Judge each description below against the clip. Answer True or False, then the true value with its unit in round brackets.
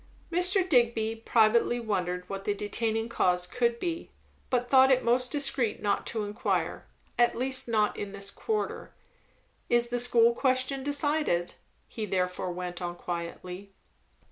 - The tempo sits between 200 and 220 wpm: False (145 wpm)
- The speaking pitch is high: True (230 Hz)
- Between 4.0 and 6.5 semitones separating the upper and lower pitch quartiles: True (4.6 semitones)